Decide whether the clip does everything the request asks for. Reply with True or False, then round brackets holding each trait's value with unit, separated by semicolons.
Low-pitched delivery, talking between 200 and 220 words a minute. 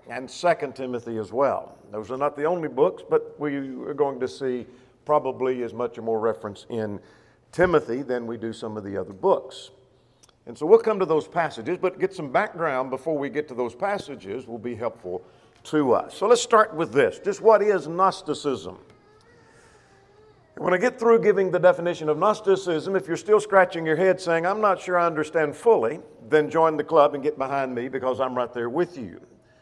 False (150 Hz; 205 wpm)